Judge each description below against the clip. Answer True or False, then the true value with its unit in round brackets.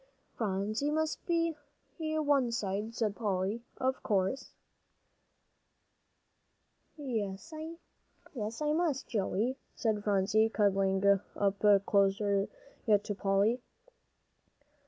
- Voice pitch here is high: True (215 Hz)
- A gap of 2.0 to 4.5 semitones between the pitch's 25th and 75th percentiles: False (5.3 semitones)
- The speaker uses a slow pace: True (85 wpm)